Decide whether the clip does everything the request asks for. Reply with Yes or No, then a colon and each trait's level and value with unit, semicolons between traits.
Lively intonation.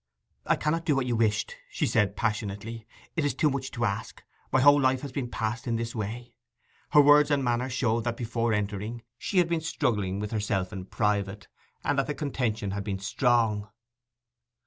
No: average, 4.3 semitones